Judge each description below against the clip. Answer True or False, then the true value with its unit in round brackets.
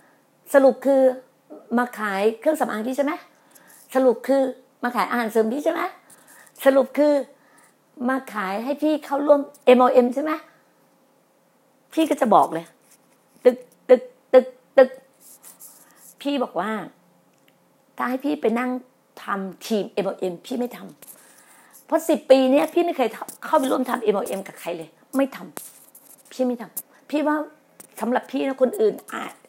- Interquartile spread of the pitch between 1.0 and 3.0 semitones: True (2.5 semitones)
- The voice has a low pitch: False (260 Hz)